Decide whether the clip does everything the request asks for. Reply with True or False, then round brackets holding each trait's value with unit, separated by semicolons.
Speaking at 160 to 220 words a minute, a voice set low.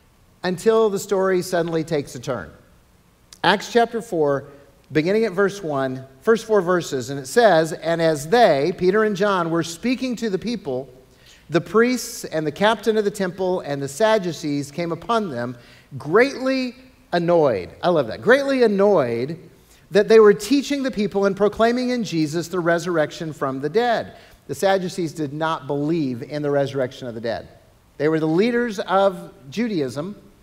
False (165 wpm; 175 Hz)